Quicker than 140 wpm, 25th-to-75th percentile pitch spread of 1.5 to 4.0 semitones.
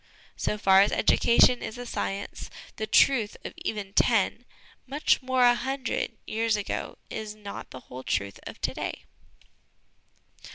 Yes: average, 155 wpm; average, 3.5 semitones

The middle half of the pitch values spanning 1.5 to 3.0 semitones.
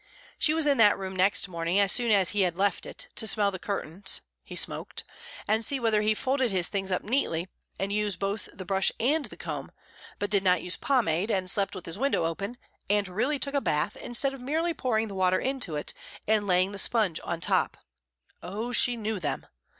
No: average, 4.3 semitones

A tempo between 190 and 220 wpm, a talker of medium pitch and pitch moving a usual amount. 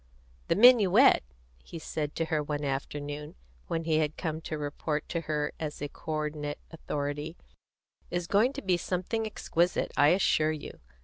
No: average, 165 wpm; medium, 155 Hz; average, 3.1 semitones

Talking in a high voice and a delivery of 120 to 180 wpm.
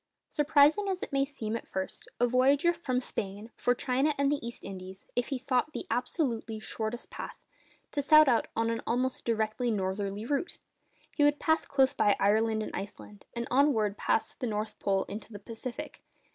No: high, 240 Hz; average, 190 wpm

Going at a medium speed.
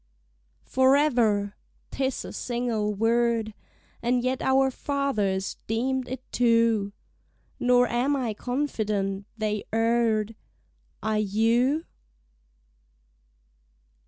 No: slow, 85 wpm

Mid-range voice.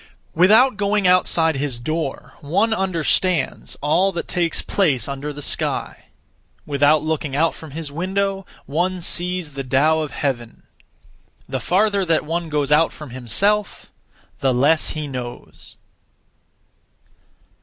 Yes: medium, 160 Hz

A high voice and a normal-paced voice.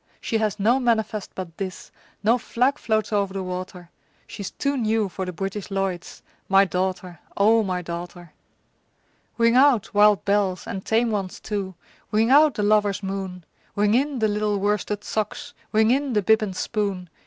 Yes: high, 205 Hz; average, 170 wpm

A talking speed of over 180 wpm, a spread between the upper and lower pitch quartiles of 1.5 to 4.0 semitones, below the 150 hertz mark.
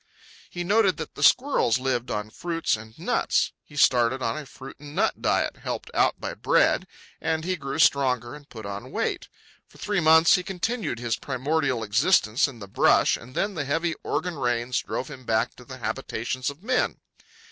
No: average, 190 wpm; wide, 5.5 semitones; medium, 140 Hz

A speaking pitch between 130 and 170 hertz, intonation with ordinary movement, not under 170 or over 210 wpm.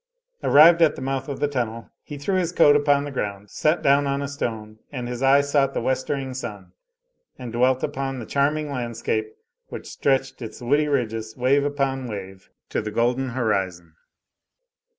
Yes: low, 135 Hz; average, 3.4 semitones; average, 175 wpm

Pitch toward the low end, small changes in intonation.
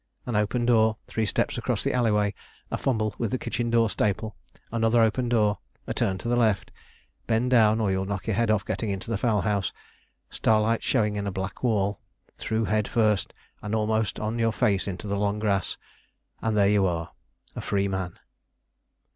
Yes: low, 110 Hz; narrow, 2.2 semitones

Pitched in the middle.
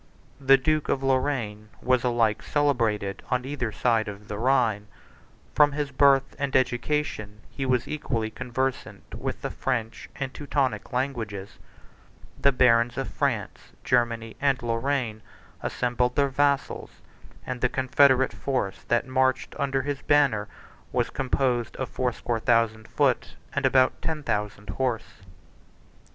No: low, 125 Hz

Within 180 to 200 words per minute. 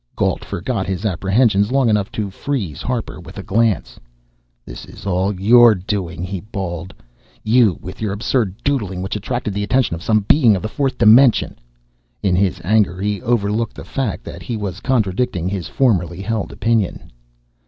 No: average, 170 wpm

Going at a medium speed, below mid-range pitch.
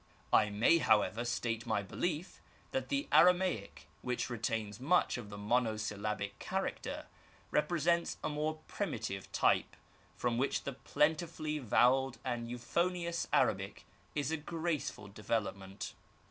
No: slow, 130 wpm; low, 125 Hz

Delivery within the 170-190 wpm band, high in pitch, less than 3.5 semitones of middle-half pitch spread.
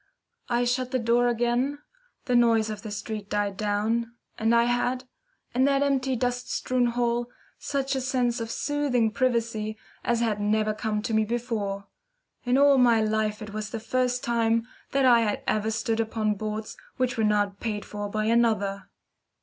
Yes: average, 175 wpm; high, 230 Hz; narrow, 2.4 semitones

